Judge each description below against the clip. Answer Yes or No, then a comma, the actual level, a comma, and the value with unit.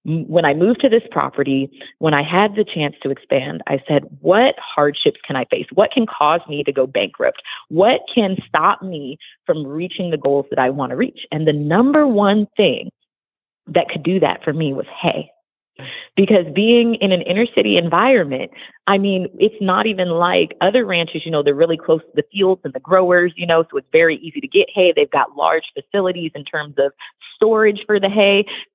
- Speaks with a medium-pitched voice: Yes, medium, 180 Hz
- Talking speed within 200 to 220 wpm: Yes, fast, 205 wpm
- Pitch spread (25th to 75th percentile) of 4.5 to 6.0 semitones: Yes, average, 5.2 semitones